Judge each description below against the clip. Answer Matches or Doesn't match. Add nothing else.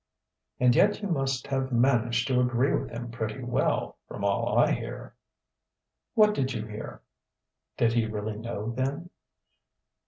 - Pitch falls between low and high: Doesn't match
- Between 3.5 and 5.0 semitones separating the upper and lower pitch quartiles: Doesn't match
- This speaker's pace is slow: Doesn't match